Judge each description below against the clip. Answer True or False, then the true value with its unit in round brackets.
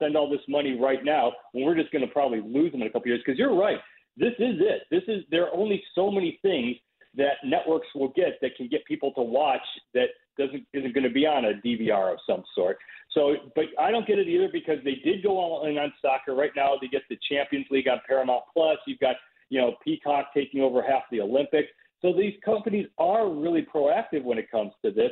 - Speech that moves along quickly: True (240 wpm)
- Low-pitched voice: False (155 Hz)